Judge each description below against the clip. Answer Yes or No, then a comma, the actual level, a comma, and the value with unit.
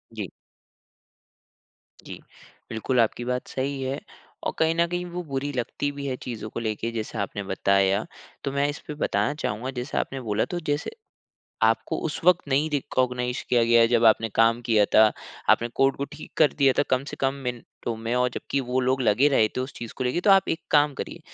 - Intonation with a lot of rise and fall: No, average, 3.5 semitones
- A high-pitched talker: No, low, 130 Hz